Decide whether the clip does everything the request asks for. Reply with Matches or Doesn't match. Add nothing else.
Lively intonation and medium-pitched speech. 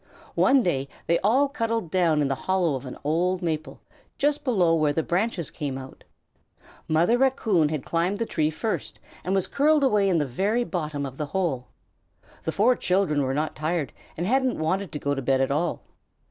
Matches